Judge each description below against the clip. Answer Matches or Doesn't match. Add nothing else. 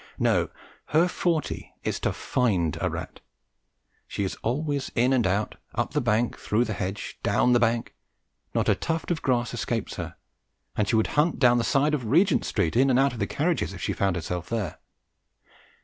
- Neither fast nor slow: Matches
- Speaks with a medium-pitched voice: Doesn't match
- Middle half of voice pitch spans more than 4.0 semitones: Matches